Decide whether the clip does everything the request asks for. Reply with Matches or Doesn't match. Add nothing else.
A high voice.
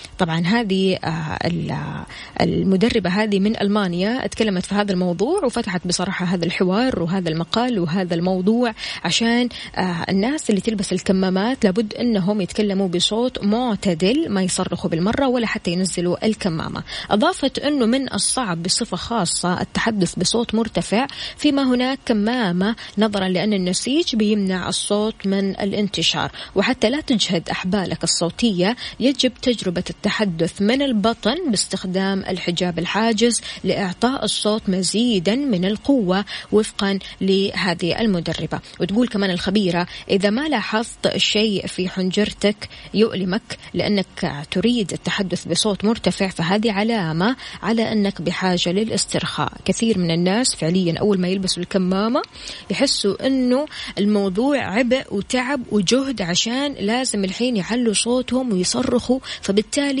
Matches